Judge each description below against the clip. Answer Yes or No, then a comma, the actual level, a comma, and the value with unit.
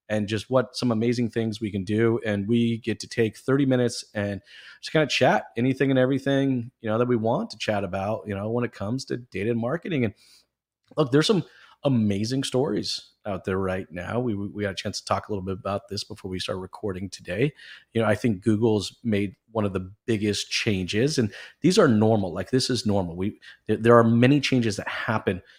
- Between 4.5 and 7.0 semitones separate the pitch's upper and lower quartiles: No, average, 3.4 semitones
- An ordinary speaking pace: No, fast, 225 wpm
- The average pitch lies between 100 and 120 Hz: Yes, low, 110 Hz